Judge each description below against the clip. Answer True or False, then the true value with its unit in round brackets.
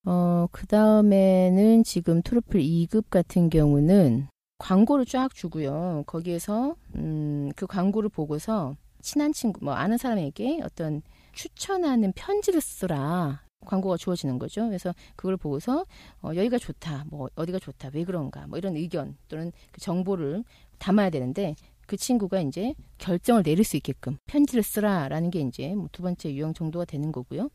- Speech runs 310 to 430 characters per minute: True (320 characters per minute)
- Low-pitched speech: False (180 Hz)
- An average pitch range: False (5.8 semitones)